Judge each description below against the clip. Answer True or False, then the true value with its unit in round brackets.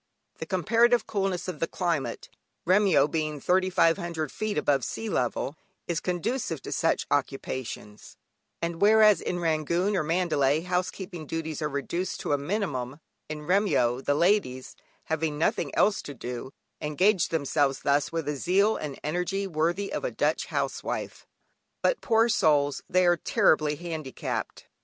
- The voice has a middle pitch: True (165 Hz)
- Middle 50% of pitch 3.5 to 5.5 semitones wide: True (4.4 semitones)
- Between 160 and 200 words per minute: False (145 wpm)